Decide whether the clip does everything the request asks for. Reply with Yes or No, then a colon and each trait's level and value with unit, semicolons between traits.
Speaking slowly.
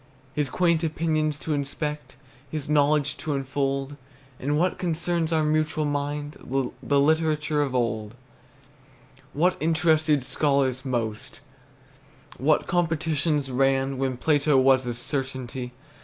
Yes: slow, 115 wpm